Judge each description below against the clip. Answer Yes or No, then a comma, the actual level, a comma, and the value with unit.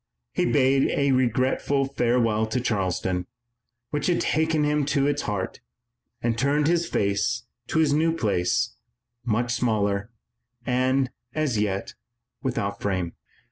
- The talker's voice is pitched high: No, low, 125 Hz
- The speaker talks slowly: Yes, slow, 130 wpm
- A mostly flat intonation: No, average, 5.1 semitones